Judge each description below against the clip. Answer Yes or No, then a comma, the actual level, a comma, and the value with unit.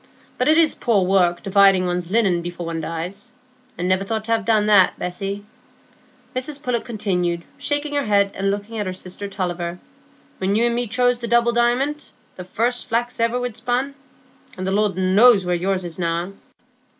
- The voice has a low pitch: No, high, 205 Hz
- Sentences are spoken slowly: No, average, 180 wpm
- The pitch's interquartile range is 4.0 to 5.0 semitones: Yes, average, 4.6 semitones